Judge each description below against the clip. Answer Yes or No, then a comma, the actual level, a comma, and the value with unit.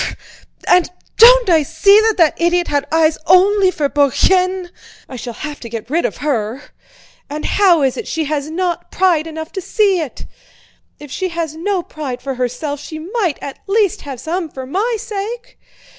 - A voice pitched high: Yes, very high, 325 Hz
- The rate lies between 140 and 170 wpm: No, average, 190 wpm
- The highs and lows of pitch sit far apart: No, average, 4.7 semitones